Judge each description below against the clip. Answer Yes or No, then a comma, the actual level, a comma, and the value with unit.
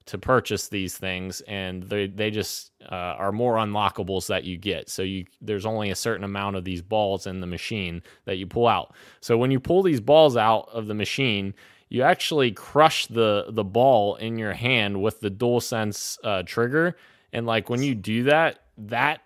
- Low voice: Yes, low, 105 Hz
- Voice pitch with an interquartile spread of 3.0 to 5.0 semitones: Yes, average, 3.4 semitones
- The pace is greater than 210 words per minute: No, average, 200 wpm